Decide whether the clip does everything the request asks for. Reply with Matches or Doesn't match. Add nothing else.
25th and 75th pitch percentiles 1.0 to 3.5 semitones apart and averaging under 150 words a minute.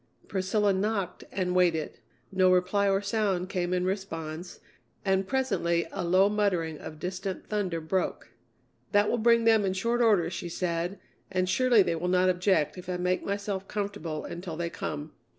Doesn't match